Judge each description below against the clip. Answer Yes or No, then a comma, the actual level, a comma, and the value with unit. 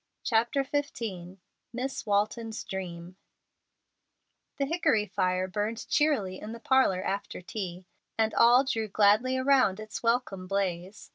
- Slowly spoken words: Yes, slow, 125 wpm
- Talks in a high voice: Yes, high, 215 Hz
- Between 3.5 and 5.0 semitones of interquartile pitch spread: Yes, average, 4.6 semitones